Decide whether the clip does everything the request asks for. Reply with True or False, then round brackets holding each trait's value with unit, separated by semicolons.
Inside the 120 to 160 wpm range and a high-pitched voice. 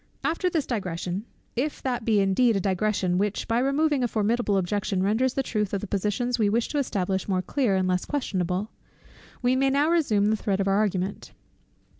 False (195 wpm; 210 Hz)